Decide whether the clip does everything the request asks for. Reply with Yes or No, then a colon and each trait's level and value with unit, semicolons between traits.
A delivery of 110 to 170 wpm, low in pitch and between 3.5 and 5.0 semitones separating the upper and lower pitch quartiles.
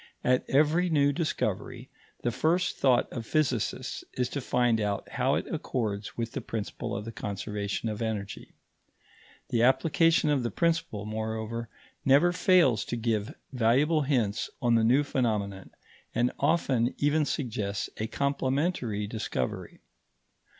Yes: slow, 135 wpm; low, 120 Hz; average, 4.6 semitones